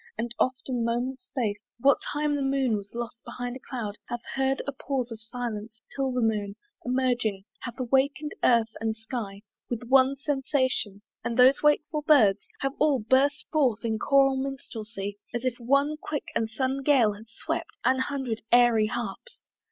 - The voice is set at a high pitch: Yes, very high, 250 Hz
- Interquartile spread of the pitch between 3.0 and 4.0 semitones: Yes, average, 3.3 semitones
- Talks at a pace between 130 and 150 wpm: No, average, 170 wpm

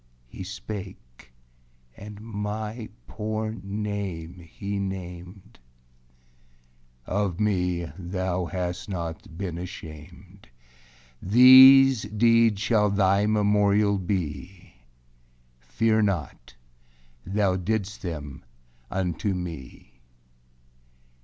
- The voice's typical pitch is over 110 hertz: No, low, 100 Hz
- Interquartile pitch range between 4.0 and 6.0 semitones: No, average, 3.2 semitones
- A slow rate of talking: Yes, slow, 80 wpm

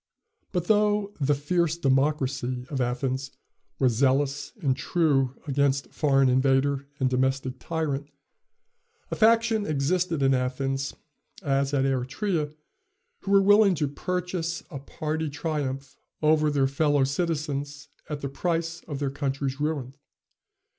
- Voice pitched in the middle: Yes, medium, 145 Hz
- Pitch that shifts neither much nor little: Yes, average, 3.2 semitones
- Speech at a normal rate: No, slow, 125 wpm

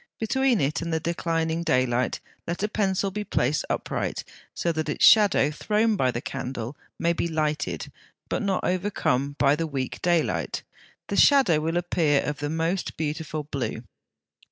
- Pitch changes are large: No, average, 4.1 semitones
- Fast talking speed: No, average, 160 wpm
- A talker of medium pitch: Yes, medium, 160 Hz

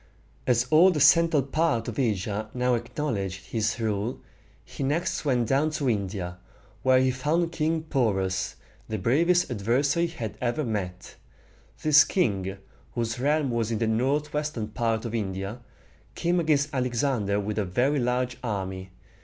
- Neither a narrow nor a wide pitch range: No, wide, 5.7 semitones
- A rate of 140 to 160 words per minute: Yes, average, 150 wpm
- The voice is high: No, low, 120 Hz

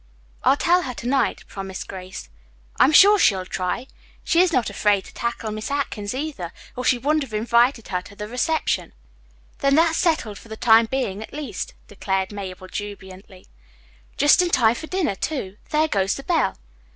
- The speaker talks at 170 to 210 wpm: Yes, average, 180 wpm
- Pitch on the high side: Yes, high, 230 Hz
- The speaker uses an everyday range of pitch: No, wide, 6.7 semitones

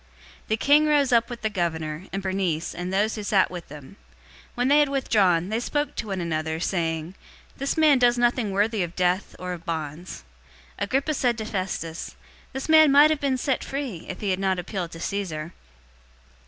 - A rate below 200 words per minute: No, fast, 205 wpm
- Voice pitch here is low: No, high, 195 Hz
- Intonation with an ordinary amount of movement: No, wide, 6.3 semitones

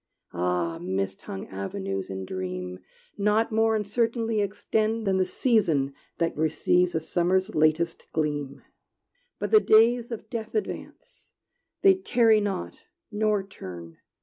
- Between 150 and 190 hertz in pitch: Yes, medium, 185 Hz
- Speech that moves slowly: Yes, slow, 125 wpm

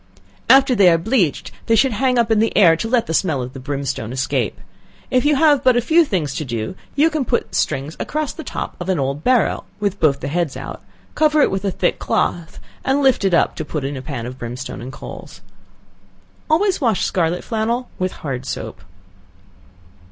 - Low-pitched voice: No, medium, 185 Hz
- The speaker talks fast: Yes, fast, 210 wpm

